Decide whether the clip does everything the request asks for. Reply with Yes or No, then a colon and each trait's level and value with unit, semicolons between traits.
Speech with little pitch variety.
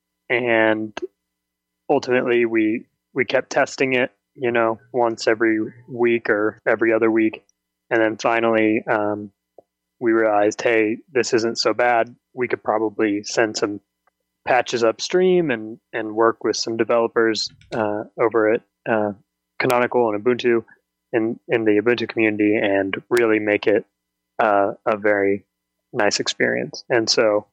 Yes: narrow, 2.1 semitones